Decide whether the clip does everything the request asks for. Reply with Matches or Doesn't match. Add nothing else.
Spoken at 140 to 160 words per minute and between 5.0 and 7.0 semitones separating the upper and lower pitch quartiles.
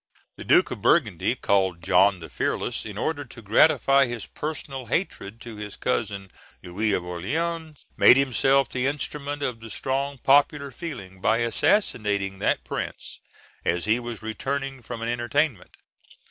Matches